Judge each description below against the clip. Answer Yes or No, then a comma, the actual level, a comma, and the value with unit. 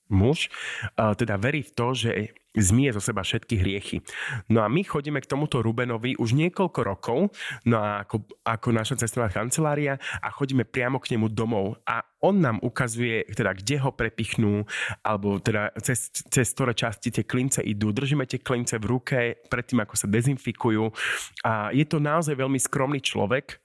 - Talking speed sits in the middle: No, fast, 170 wpm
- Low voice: Yes, low, 120 Hz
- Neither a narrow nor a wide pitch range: Yes, average, 3.4 semitones